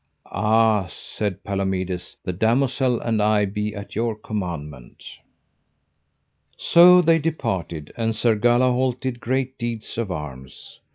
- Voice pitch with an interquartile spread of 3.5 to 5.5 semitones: Yes, average, 4.4 semitones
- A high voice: No, low, 110 Hz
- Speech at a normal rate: No, slow, 120 wpm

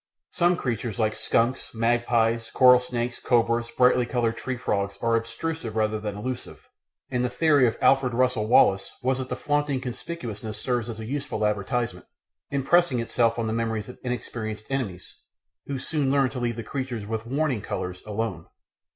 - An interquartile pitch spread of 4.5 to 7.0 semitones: No, average, 2.8 semitones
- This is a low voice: Yes, low, 120 Hz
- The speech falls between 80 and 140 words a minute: No, average, 165 wpm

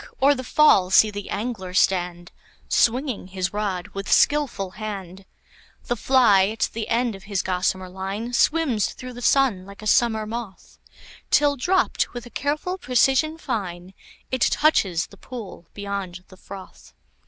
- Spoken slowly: No, average, 155 wpm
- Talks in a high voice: Yes, high, 215 Hz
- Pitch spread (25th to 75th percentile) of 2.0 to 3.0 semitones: No, average, 4.9 semitones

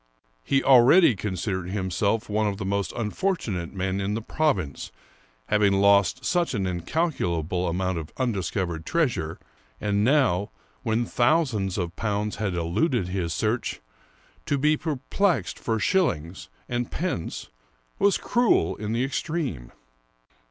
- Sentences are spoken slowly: Yes, slow, 130 wpm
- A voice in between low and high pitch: No, low, 105 Hz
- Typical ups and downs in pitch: No, wide, 6.3 semitones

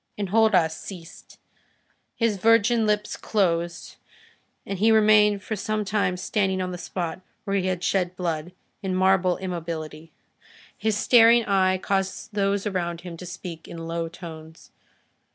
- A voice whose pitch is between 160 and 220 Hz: Yes, medium, 185 Hz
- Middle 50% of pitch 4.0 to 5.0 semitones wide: No, average, 3.3 semitones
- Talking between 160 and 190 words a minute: No, average, 140 wpm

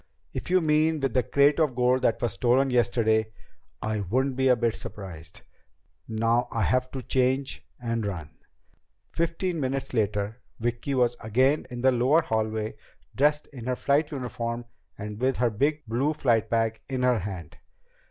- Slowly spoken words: No, average, 160 wpm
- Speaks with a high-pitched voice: No, low, 125 Hz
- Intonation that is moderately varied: Yes, average, 3.4 semitones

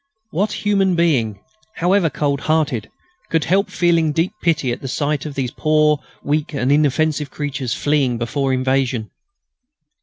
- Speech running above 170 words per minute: No, average, 145 wpm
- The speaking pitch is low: No, medium, 150 Hz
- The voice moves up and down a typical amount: Yes, average, 3.5 semitones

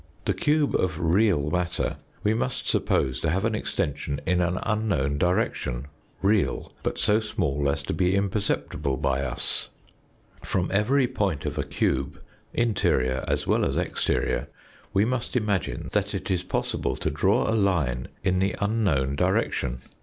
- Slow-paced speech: No, average, 155 wpm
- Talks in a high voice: No, very low, 90 Hz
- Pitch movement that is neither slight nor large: No, wide, 6.8 semitones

